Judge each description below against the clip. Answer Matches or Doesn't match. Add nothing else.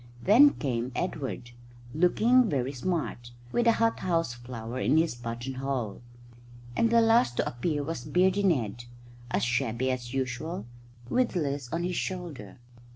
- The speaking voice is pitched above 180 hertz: Doesn't match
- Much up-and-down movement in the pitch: Matches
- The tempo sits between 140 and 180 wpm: Matches